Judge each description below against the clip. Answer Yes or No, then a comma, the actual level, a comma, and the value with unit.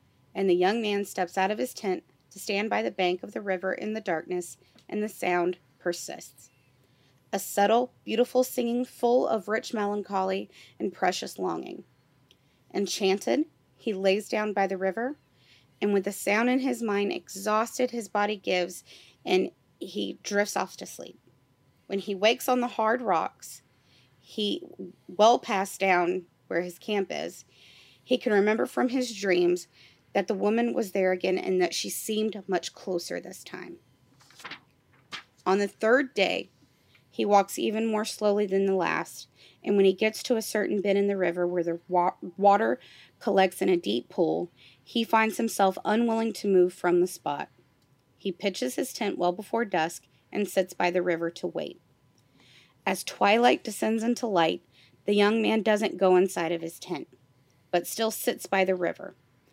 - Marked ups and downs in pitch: No, average, 4.0 semitones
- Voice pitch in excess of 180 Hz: Yes, high, 190 Hz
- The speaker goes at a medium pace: Yes, average, 170 wpm